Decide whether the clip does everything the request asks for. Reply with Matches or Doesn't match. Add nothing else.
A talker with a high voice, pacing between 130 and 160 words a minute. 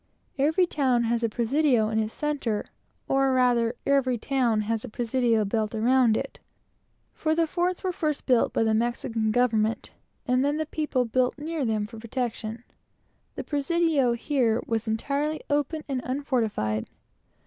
Matches